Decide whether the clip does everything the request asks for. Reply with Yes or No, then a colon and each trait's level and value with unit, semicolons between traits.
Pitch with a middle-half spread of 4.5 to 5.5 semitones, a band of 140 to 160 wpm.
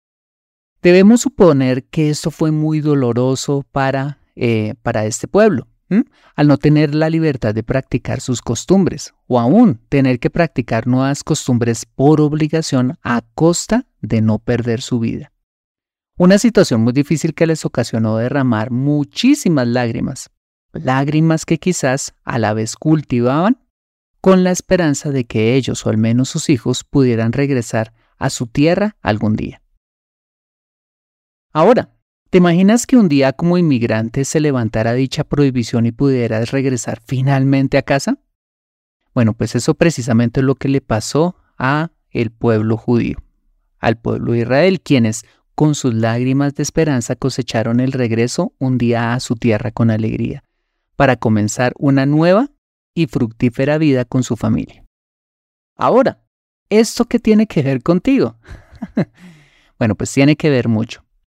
Yes: average, 5.2 semitones; average, 145 wpm